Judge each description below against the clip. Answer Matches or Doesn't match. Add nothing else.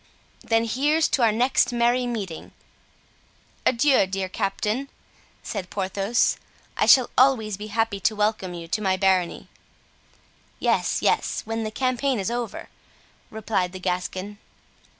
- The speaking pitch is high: Matches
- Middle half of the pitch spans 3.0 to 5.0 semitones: Matches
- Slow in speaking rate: Matches